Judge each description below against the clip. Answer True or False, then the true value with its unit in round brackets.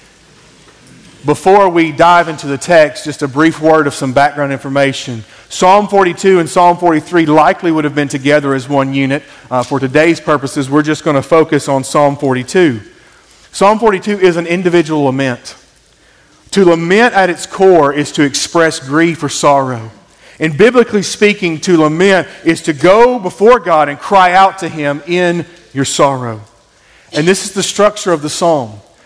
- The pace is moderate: True (170 wpm)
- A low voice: False (160 Hz)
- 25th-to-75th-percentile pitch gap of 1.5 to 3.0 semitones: False (4.2 semitones)